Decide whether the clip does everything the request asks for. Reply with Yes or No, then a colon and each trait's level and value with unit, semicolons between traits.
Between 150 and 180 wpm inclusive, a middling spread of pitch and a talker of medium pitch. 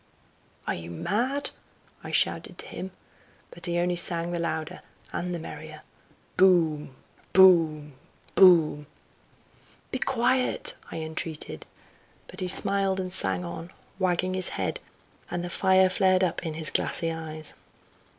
No: slow, 135 wpm; average, 3.0 semitones; medium, 175 Hz